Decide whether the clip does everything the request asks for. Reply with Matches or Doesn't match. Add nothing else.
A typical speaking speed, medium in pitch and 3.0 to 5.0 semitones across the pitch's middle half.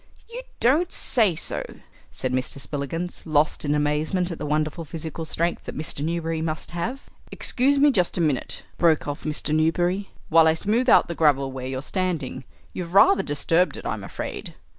Matches